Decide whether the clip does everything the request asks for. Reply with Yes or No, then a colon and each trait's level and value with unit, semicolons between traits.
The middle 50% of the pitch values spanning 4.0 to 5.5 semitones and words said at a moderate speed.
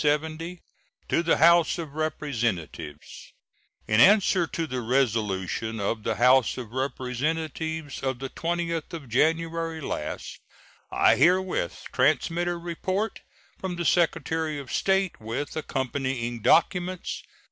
No: average, 5.0 semitones; slow, 115 wpm